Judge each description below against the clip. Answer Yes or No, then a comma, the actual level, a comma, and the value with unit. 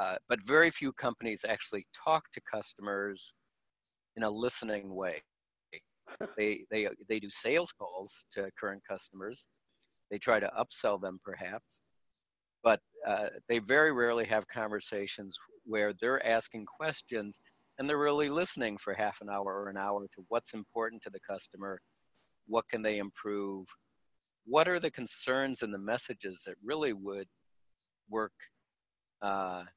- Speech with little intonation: No, average, 3.4 semitones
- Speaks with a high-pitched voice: No, low, 110 Hz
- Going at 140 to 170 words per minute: Yes, average, 150 wpm